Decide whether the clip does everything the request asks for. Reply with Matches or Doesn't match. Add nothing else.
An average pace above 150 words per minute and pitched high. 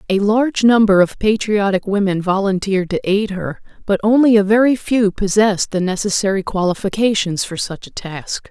Matches